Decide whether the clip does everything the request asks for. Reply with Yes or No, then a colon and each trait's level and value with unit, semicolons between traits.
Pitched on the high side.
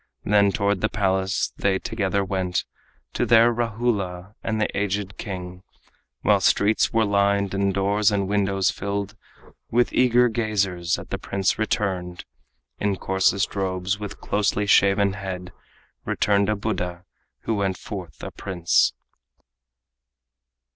No: low, 100 Hz